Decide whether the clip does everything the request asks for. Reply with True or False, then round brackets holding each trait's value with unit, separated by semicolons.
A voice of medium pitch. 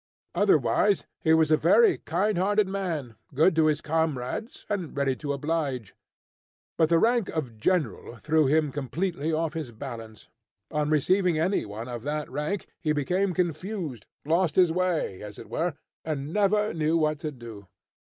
True (155 Hz)